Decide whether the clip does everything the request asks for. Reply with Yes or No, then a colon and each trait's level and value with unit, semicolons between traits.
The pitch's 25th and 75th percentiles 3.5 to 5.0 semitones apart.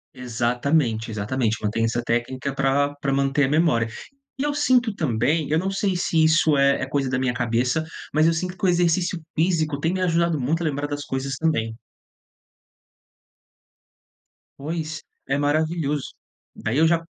Yes: average, 4.2 semitones